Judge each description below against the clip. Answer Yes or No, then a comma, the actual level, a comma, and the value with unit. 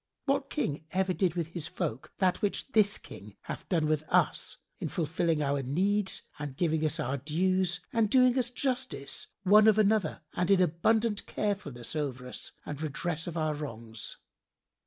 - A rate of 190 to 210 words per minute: No, average, 170 wpm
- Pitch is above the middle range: No, medium, 170 Hz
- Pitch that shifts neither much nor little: No, wide, 5.7 semitones